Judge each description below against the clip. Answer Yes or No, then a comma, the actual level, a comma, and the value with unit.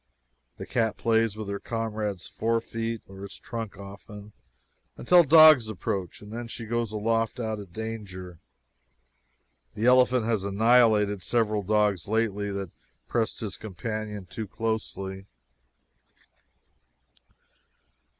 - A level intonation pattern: Yes, narrow, 2.2 semitones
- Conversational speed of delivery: No, slow, 115 wpm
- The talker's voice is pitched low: Yes, low, 110 Hz